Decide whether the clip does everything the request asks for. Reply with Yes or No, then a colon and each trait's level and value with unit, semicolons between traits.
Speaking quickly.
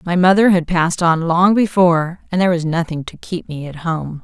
Yes: fast, 225 wpm